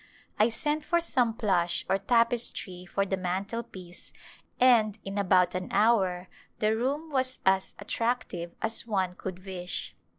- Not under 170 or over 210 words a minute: No, average, 140 wpm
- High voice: Yes, high, 200 Hz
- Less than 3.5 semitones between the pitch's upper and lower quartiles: No, average, 4.3 semitones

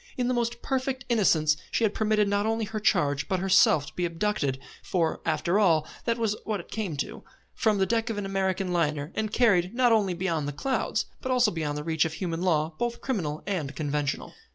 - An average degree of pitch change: No, wide, 5.7 semitones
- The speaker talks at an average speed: No, fast, 215 wpm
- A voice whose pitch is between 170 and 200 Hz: Yes, high, 190 Hz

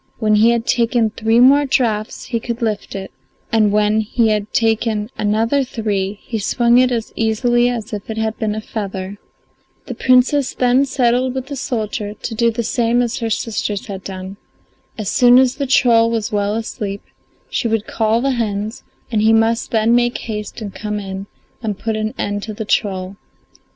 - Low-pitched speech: No, high, 225 Hz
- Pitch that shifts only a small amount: Yes, narrow, 2.3 semitones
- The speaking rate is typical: Yes, average, 190 wpm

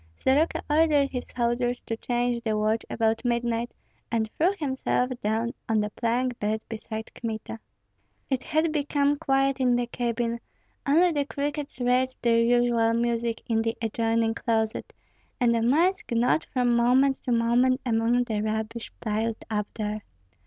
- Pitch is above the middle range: Yes, high, 235 Hz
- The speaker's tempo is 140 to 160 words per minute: Yes, average, 150 wpm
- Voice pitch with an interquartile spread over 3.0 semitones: No, narrow, 2.4 semitones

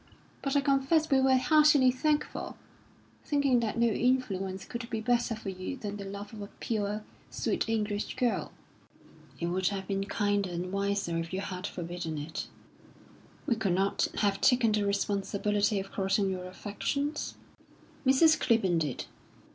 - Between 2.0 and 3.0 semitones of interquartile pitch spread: No, average, 4.5 semitones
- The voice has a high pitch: Yes, high, 205 Hz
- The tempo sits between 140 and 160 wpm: Yes, average, 155 wpm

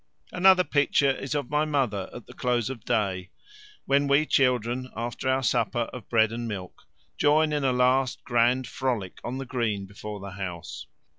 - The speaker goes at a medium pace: Yes, average, 180 wpm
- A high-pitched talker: No, low, 125 Hz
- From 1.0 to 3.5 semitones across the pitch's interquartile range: No, average, 3.9 semitones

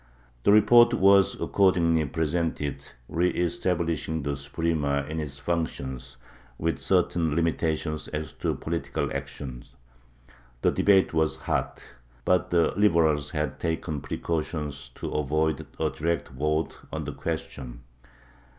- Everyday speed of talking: No, slow, 120 wpm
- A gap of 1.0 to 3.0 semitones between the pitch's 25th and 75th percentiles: Yes, narrow, 2.6 semitones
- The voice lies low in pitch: Yes, very low, 80 Hz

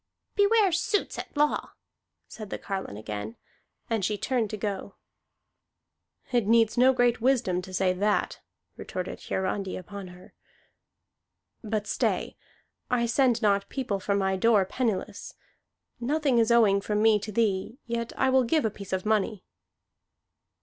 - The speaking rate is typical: Yes, average, 145 wpm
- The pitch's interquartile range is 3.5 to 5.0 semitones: Yes, average, 3.8 semitones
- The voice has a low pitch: No, high, 215 Hz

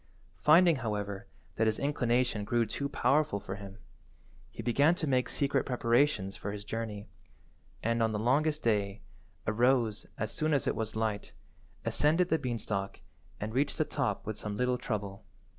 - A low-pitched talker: Yes, low, 115 Hz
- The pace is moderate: Yes, average, 160 wpm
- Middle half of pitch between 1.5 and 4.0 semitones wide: No, average, 5.0 semitones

